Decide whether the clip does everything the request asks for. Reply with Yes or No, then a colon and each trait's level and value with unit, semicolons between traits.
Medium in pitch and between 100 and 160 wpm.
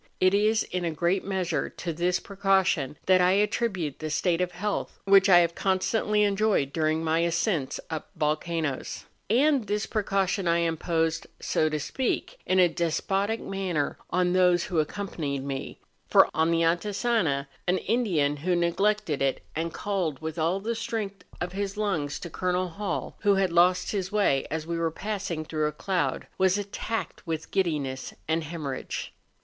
No: medium, 180 Hz; average, 175 wpm